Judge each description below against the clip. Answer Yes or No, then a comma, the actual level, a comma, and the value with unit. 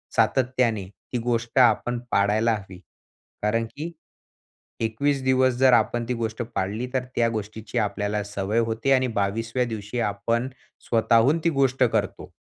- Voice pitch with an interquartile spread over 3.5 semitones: No, average, 3.0 semitones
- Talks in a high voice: No, low, 115 Hz